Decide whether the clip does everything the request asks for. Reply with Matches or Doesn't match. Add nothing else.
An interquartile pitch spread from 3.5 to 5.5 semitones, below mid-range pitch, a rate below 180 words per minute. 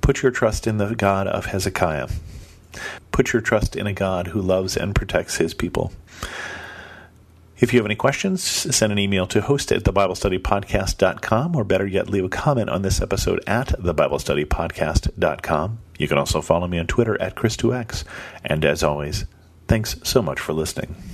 Matches